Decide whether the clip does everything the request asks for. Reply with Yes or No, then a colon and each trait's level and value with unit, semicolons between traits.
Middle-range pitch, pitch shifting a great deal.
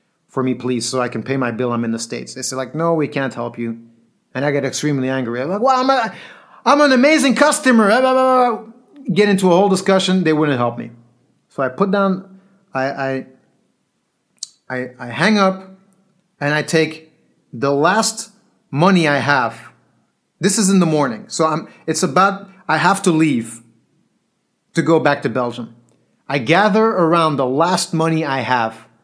Yes: medium, 160 Hz; wide, 7.1 semitones